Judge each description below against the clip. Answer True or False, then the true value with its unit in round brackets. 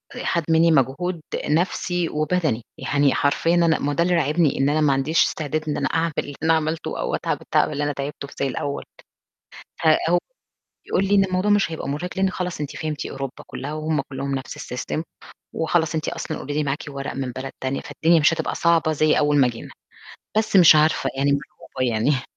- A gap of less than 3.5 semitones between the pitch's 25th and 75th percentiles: True (3.1 semitones)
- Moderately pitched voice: True (155 Hz)